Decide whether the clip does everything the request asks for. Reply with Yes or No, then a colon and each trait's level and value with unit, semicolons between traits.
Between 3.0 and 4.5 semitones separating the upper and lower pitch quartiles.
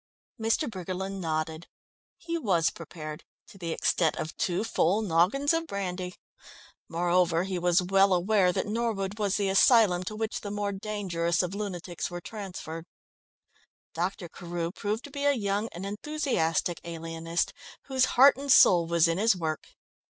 Yes: average, 3.8 semitones